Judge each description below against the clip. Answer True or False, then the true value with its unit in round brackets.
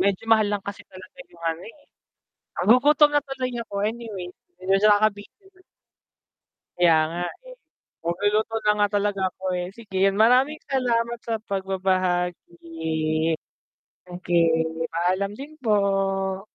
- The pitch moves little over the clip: False (4.4 semitones)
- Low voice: False (200 Hz)